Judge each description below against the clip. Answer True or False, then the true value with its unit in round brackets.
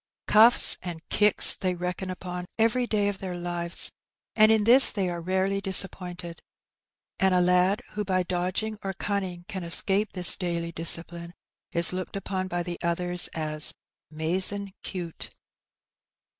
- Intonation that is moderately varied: False (2.2 semitones)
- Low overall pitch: False (185 Hz)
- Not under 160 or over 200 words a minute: False (145 wpm)